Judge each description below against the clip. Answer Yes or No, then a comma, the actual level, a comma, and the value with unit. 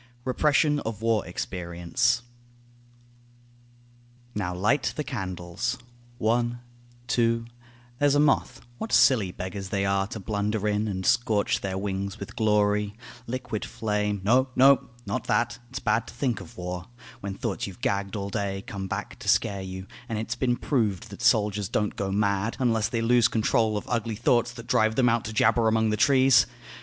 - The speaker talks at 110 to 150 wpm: No, average, 170 wpm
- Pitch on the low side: Yes, low, 110 Hz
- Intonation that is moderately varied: Yes, average, 3.3 semitones